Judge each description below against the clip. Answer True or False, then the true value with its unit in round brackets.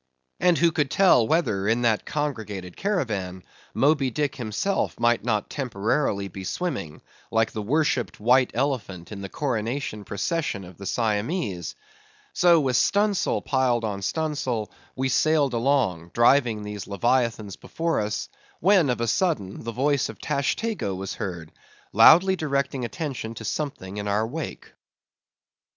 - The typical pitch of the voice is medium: False (120 Hz)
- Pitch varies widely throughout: True (6.1 semitones)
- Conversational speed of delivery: True (145 wpm)